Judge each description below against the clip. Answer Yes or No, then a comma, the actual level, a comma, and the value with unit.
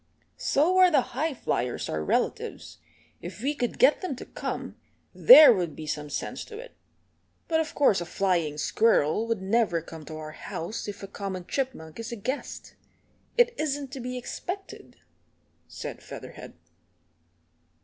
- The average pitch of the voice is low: No, high, 230 Hz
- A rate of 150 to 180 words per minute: Yes, average, 160 wpm